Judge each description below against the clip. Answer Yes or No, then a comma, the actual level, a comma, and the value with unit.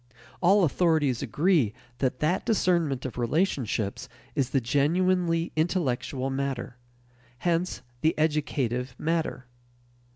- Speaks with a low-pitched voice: No, medium, 150 Hz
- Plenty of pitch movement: No, average, 5.0 semitones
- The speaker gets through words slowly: Yes, slow, 100 wpm